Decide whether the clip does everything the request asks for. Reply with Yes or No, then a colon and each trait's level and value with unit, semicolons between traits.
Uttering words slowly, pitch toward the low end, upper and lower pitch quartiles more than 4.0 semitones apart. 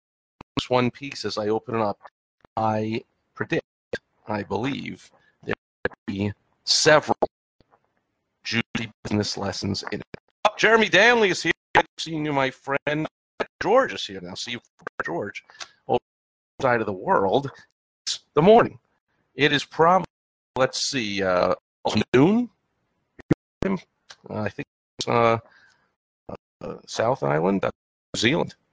Yes: slow, 130 wpm; low, 115 Hz; average, 4.6 semitones